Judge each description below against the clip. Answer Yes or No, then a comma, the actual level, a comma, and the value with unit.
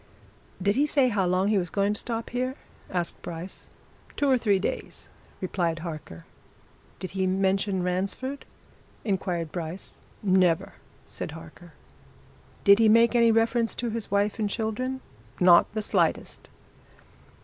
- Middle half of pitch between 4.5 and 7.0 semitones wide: No, average, 4.1 semitones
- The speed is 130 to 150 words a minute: Yes, average, 140 wpm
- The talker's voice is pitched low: No, high, 200 Hz